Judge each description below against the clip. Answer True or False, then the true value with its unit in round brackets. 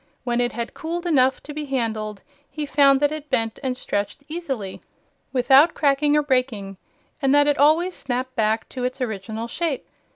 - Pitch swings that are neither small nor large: True (4.1 semitones)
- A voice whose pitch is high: True (265 Hz)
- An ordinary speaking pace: True (175 wpm)